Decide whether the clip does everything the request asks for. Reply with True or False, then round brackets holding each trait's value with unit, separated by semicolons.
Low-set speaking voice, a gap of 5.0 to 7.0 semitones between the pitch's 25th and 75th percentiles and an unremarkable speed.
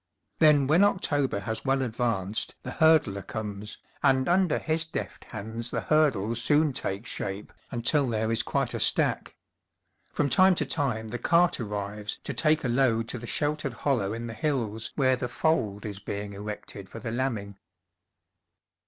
True (120 Hz; 5.5 semitones; 165 wpm)